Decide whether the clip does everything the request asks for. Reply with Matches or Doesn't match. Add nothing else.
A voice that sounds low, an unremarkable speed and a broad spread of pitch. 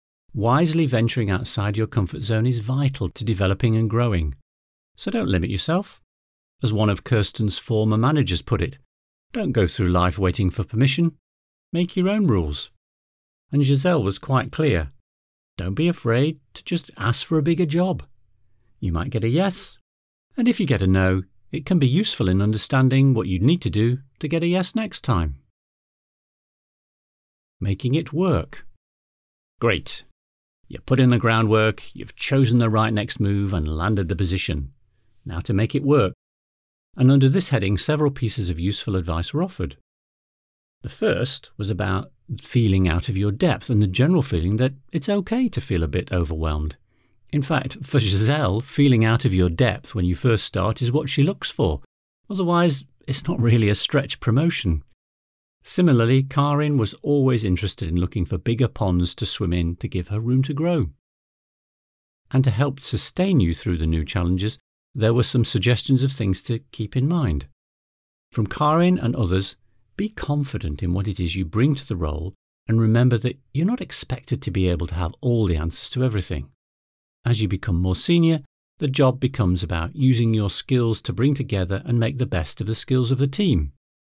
Matches